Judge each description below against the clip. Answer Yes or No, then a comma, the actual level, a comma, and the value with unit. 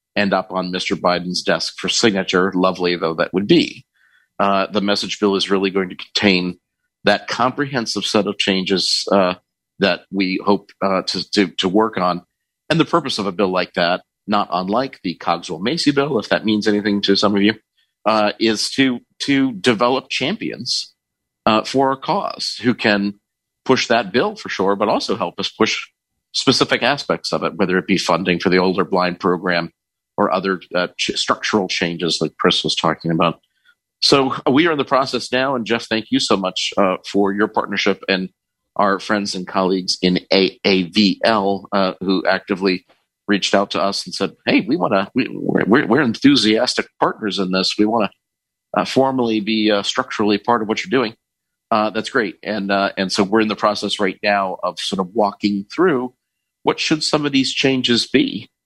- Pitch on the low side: Yes, low, 100 Hz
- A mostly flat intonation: No, average, 3.2 semitones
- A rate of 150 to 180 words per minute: No, average, 190 wpm